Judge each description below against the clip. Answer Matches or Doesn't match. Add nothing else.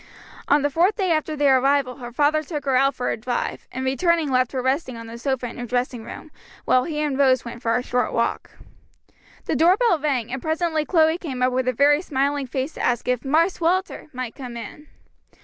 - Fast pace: Matches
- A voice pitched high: Matches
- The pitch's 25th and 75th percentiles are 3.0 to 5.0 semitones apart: Matches